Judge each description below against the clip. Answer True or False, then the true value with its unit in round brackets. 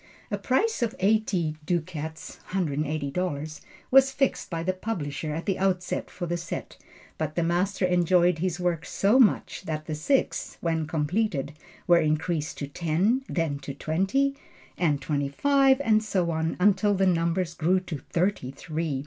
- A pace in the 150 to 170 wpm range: True (155 wpm)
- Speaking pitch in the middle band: True (175 Hz)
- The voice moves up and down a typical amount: True (3.8 semitones)